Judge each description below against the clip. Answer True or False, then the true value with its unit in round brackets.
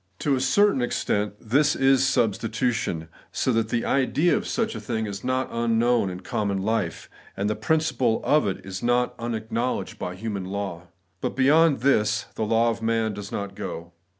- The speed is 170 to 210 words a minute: True (175 wpm)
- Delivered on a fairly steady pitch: False (4.2 semitones)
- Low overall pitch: True (115 Hz)